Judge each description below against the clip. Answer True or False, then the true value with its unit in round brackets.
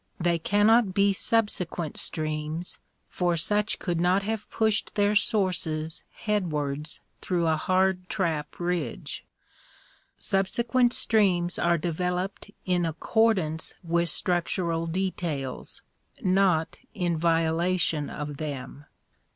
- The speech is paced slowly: True (100 wpm)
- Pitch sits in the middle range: True (175 Hz)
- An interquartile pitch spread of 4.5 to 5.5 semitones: False (3.3 semitones)